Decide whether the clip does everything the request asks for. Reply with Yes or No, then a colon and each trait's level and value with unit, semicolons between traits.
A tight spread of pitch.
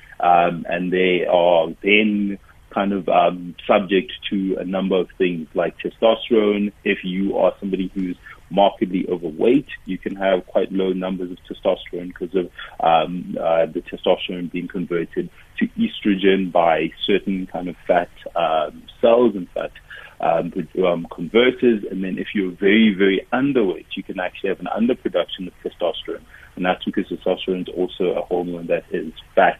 Yes: narrow, 2.2 semitones